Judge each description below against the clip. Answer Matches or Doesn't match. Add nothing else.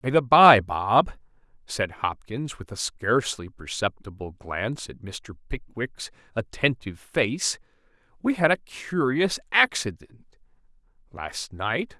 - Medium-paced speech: Doesn't match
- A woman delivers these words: Doesn't match